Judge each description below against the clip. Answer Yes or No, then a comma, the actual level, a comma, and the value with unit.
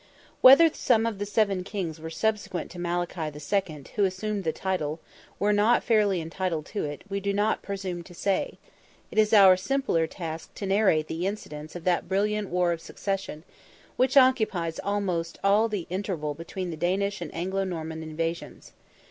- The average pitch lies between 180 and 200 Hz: Yes, high, 190 Hz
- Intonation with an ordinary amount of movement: Yes, average, 3.6 semitones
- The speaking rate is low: No, average, 170 wpm